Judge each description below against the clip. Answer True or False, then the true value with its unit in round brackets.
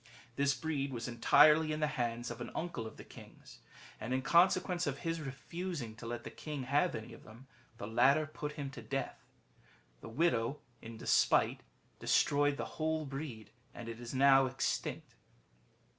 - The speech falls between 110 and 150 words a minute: False (175 wpm)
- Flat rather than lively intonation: False (4.4 semitones)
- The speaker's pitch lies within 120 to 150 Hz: True (140 Hz)